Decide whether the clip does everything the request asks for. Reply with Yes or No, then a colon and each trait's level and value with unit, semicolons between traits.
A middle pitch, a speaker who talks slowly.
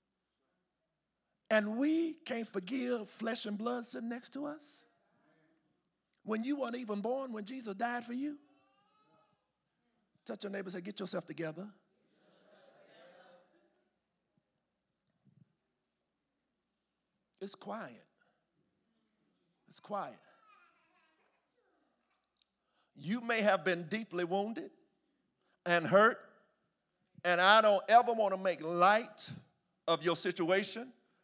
No: high, 210 Hz; slow, 100 wpm